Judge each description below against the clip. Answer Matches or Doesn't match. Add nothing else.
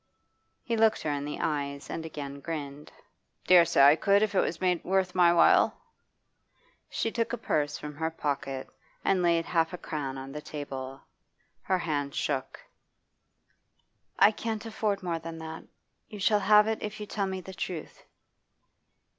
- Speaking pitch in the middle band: Matches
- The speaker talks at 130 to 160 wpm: Doesn't match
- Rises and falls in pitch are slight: Doesn't match